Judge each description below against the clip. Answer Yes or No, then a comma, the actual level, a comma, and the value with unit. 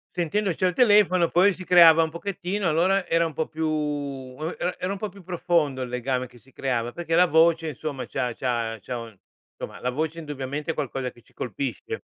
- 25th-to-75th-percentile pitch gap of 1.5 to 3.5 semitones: No, wide, 5.4 semitones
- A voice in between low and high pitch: Yes, medium, 160 Hz